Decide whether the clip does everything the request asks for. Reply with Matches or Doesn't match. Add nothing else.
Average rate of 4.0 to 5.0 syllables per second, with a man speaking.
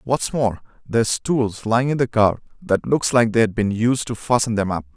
Matches